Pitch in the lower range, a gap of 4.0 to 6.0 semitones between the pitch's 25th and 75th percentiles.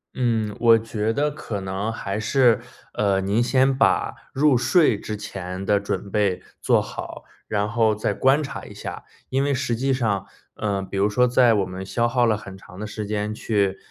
No: low, 110 Hz; average, 3.6 semitones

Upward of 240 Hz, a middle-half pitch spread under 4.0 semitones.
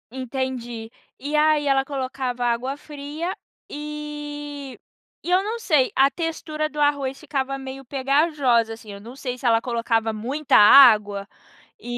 Yes: very high, 270 Hz; average, 3.5 semitones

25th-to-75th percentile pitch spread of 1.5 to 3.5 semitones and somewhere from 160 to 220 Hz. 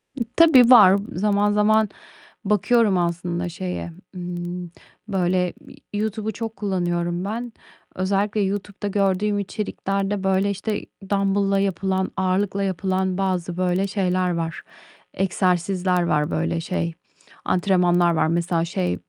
Yes: narrow, 2.4 semitones; high, 190 Hz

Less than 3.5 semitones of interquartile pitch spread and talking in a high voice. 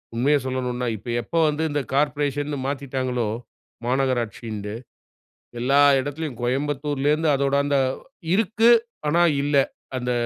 No: average, 2.8 semitones; medium, 140 Hz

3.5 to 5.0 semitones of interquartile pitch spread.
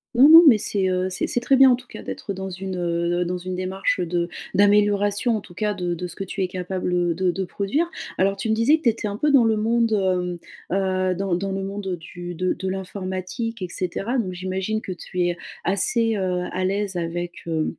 No: average, 2.9 semitones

